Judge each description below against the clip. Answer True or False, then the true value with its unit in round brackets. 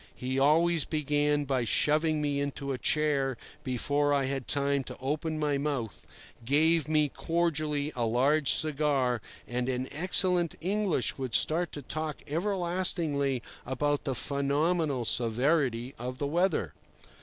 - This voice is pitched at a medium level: True (145 Hz)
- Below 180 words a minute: True (135 wpm)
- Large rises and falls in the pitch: False (2.9 semitones)